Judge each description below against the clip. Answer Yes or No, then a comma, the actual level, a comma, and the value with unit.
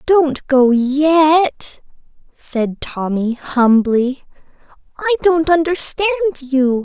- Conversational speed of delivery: No, slow, 90 wpm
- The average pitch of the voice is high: Yes, very high, 290 Hz